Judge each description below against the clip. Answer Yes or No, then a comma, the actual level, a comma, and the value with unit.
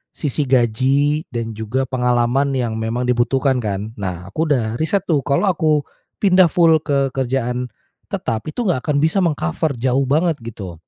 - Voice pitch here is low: Yes, low, 130 Hz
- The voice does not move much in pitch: No, average, 4.3 semitones